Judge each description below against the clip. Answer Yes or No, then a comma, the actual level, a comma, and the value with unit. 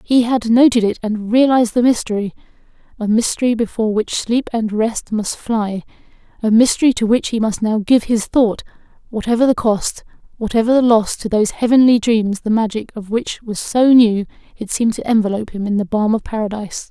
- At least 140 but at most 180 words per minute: No, average, 190 wpm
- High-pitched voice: Yes, high, 225 Hz